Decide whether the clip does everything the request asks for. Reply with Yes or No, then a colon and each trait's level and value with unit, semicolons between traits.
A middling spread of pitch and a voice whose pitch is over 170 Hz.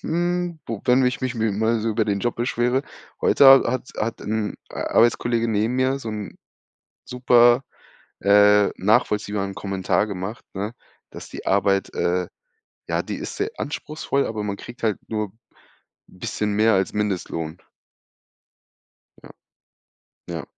No: average, 3.2 semitones; low, 110 Hz